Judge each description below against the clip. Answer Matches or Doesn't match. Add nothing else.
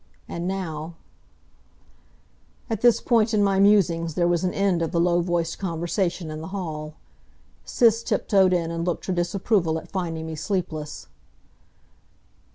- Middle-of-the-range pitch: Matches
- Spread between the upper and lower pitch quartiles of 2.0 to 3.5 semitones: Matches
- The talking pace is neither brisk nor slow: Matches